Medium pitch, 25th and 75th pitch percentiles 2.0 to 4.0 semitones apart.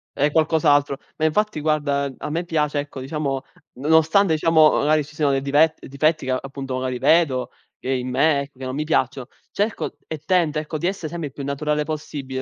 Yes: medium, 150 Hz; narrow, 2.6 semitones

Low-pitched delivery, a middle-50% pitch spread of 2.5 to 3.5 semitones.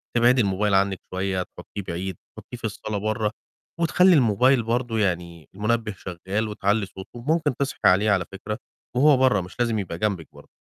No: low, 105 Hz; average, 3.9 semitones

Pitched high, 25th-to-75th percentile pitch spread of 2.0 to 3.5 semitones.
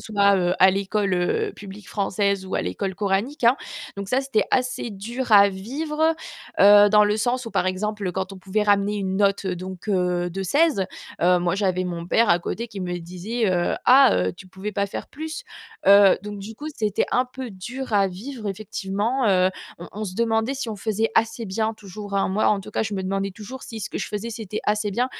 Yes: high, 205 Hz; average, 2.9 semitones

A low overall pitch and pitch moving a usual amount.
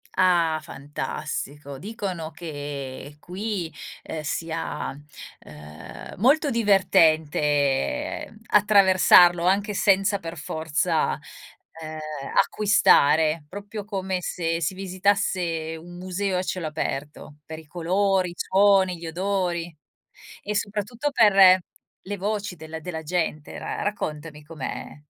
No: medium, 175 Hz; average, 4.1 semitones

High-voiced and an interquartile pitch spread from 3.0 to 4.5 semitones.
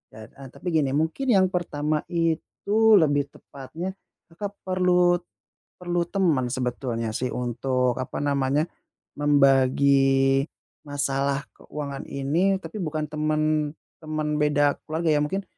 No: medium, 150 Hz; average, 3.9 semitones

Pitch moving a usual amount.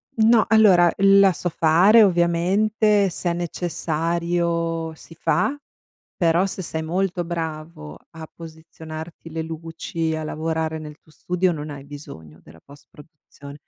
No: narrow, 2.2 semitones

